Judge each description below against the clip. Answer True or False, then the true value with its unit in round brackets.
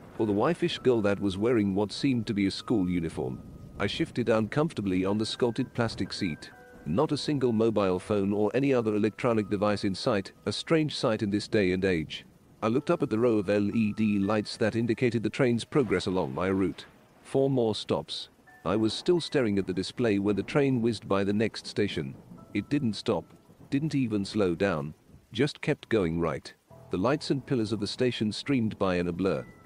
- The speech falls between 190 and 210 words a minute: True (200 wpm)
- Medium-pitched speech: False (110 Hz)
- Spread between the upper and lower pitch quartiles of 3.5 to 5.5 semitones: True (4.1 semitones)